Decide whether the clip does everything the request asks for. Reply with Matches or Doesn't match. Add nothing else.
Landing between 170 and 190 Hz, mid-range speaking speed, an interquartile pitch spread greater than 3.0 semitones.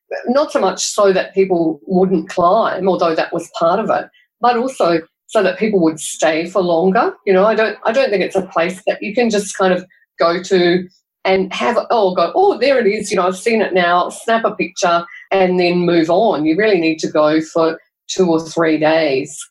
Doesn't match